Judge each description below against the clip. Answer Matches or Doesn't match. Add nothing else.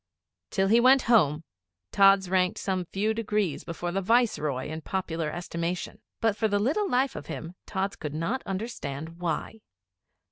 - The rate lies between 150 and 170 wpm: Matches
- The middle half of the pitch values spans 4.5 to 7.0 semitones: Matches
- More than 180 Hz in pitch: Matches